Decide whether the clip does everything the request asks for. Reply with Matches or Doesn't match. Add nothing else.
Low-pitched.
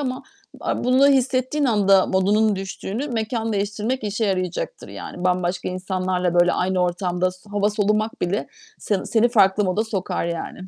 Doesn't match